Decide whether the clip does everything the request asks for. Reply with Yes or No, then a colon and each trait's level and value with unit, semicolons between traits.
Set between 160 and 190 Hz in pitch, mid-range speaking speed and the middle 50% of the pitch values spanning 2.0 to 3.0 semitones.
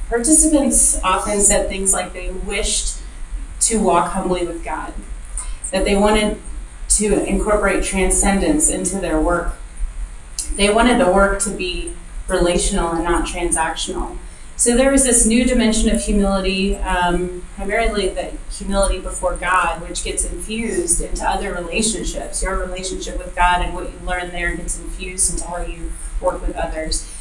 Yes: medium, 185 Hz; average, 150 wpm; average, 2.7 semitones